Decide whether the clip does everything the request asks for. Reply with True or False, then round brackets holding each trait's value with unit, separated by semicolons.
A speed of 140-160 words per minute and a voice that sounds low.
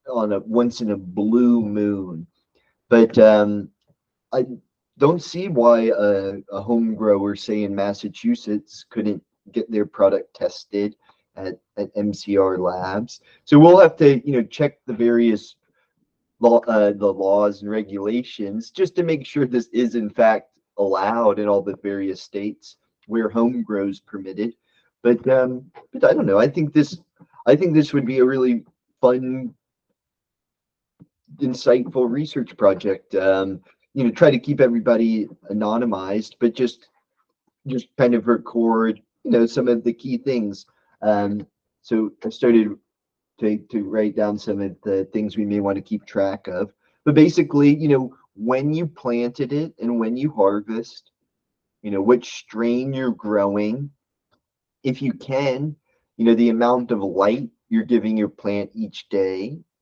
True (155 wpm; 115 Hz)